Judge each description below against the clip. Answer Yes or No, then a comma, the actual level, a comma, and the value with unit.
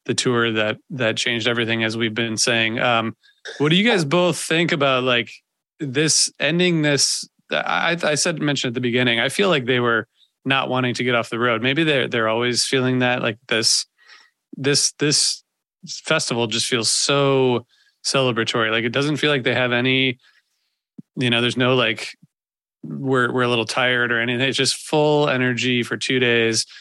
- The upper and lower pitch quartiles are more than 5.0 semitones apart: No, average, 3.3 semitones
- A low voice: Yes, low, 125 Hz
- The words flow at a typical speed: Yes, average, 185 wpm